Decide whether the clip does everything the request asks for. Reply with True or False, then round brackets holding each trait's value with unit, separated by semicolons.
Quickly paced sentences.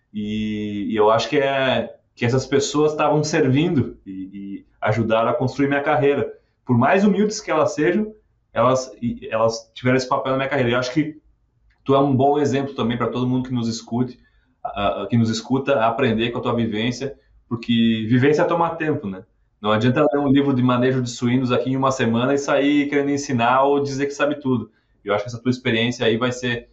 True (210 wpm)